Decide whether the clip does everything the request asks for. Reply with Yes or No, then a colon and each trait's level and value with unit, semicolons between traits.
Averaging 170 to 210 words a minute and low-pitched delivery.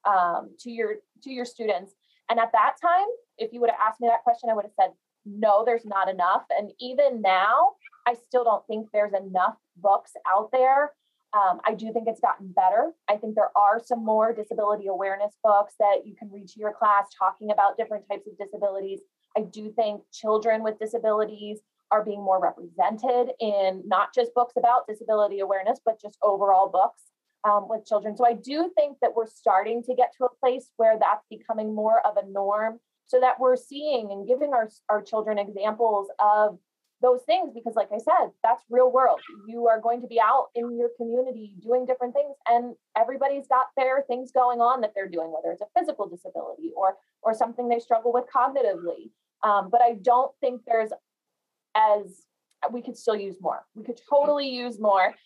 No: average, 195 wpm; high, 225 Hz